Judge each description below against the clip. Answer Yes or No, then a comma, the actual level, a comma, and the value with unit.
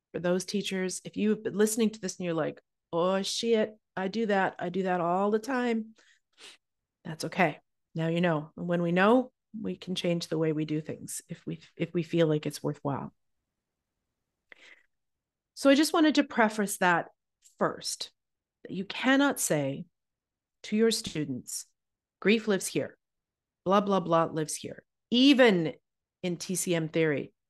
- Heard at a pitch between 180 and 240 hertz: Yes, medium, 185 Hz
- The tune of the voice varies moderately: Yes, average, 4.7 semitones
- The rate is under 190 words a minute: Yes, average, 160 wpm